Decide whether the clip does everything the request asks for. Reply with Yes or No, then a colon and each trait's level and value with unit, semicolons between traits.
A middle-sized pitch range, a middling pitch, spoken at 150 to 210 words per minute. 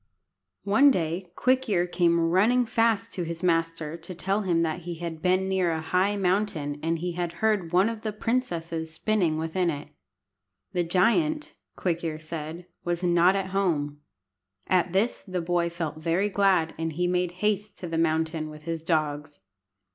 Yes: average, 3.0 semitones; medium, 175 Hz; average, 170 wpm